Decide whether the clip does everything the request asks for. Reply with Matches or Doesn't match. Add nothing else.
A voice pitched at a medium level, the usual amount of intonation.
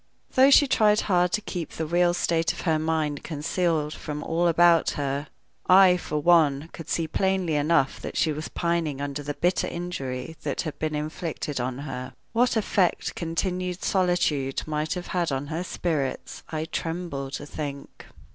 Matches